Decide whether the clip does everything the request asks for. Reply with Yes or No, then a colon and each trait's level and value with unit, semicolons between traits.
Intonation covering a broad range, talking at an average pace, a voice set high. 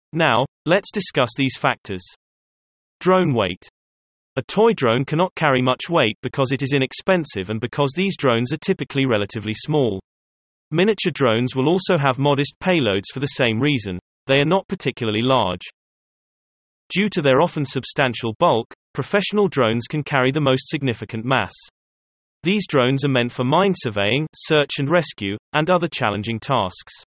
No: wide, 5.9 semitones; average, 155 wpm; low, 135 Hz